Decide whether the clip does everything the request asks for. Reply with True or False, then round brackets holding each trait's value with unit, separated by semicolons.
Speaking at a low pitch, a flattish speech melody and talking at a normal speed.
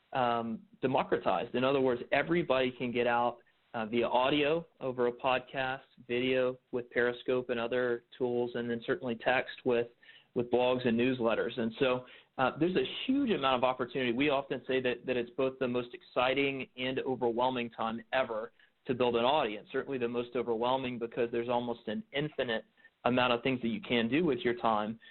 True (125 Hz; 1.5 semitones; 180 wpm)